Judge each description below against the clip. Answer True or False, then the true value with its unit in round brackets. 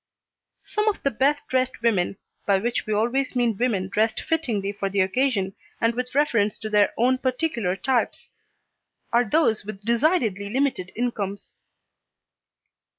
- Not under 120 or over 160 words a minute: True (145 wpm)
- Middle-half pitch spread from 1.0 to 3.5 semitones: False (4.3 semitones)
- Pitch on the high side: True (230 Hz)